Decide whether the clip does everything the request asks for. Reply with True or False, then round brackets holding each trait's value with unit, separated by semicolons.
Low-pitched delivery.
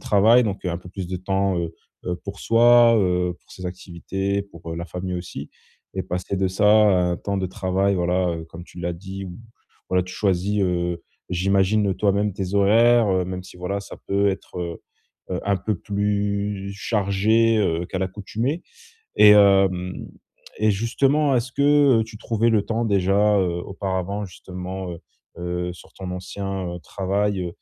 True (95 Hz)